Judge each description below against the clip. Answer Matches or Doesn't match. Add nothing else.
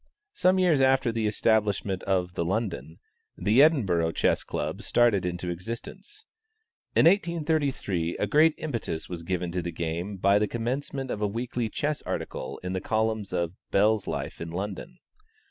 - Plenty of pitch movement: Matches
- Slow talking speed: Doesn't match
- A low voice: Matches